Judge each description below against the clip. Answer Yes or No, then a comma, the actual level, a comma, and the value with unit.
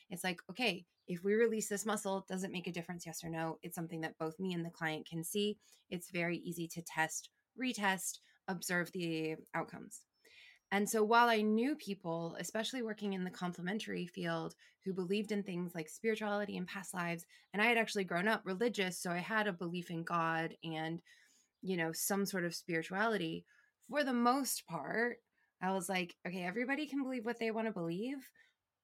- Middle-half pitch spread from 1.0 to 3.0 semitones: No, average, 4.3 semitones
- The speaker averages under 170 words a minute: No, average, 195 wpm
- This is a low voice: No, high, 190 Hz